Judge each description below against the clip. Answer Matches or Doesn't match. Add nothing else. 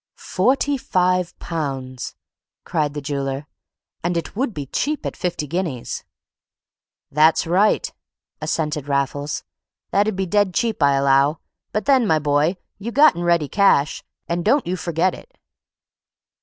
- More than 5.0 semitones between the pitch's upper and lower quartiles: Matches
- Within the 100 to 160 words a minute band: Matches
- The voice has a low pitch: Doesn't match